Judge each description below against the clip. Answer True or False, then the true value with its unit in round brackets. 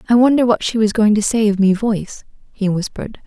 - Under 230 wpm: False (240 wpm)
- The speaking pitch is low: False (215 Hz)